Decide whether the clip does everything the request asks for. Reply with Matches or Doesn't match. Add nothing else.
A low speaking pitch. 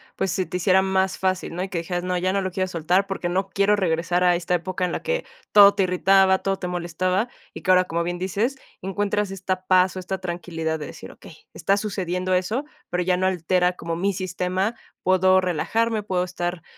Doesn't match